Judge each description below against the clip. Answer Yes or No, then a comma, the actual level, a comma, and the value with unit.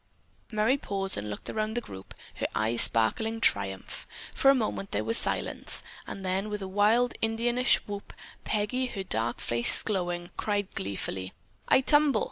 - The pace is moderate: Yes, average, 160 wpm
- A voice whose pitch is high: Yes, high, 205 Hz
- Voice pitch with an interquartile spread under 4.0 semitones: No, average, 4.6 semitones